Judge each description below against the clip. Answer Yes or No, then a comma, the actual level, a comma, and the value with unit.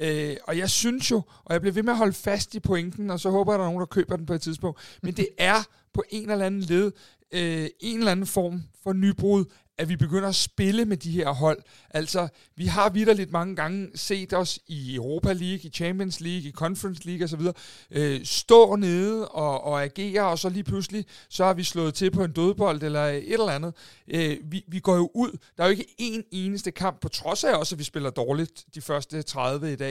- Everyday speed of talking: No, fast, 230 wpm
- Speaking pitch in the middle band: Yes, medium, 180 Hz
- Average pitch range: Yes, average, 3.9 semitones